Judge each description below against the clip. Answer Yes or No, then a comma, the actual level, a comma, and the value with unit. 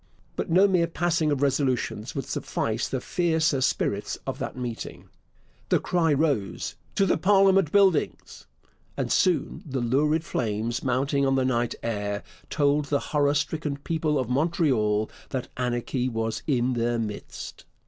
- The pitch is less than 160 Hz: Yes, medium, 140 Hz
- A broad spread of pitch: No, average, 4.9 semitones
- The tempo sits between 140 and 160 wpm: Yes, average, 150 wpm